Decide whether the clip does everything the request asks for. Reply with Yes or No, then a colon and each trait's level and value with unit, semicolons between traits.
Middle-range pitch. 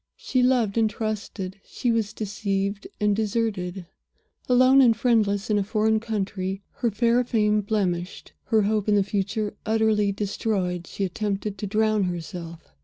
No: high, 210 Hz